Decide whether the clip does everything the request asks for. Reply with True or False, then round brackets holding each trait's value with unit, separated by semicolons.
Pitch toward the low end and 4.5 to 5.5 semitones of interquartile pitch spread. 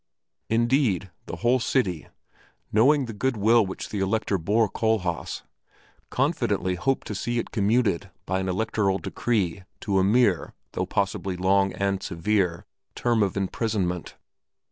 False (100 Hz; 3.4 semitones)